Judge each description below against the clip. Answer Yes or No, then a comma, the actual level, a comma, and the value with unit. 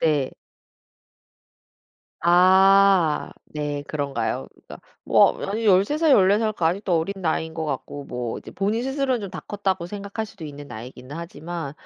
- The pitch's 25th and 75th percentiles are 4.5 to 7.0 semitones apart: Yes, wide, 5.4 semitones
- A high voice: No, medium, 175 Hz